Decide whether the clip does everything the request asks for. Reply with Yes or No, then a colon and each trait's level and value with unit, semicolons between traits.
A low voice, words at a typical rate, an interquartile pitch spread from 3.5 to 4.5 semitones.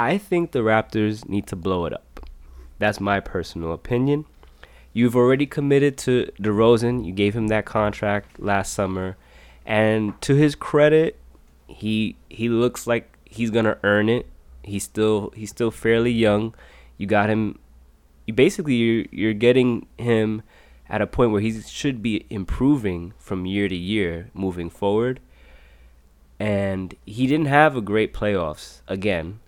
Yes: low, 105 Hz; average, 150 wpm; average, 4.1 semitones